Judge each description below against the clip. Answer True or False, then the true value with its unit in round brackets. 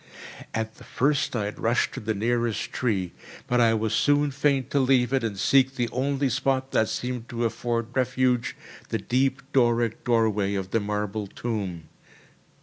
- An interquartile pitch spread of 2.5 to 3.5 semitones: True (3.0 semitones)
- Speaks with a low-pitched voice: True (120 Hz)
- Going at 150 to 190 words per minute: True (170 wpm)